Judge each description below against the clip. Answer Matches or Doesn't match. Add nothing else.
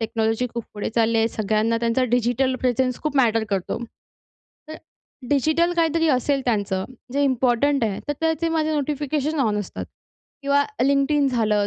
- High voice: Matches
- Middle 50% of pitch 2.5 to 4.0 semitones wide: Doesn't match